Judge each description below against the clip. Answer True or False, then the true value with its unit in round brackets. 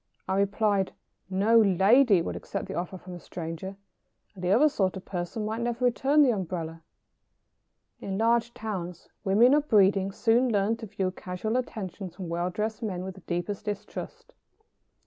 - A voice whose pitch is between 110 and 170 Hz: False (200 Hz)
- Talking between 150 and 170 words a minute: True (165 wpm)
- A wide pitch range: False (3.6 semitones)